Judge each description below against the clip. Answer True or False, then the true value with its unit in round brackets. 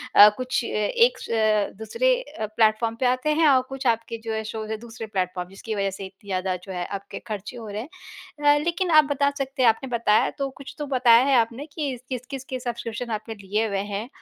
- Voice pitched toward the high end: True (230 Hz)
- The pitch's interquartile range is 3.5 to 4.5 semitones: True (4.0 semitones)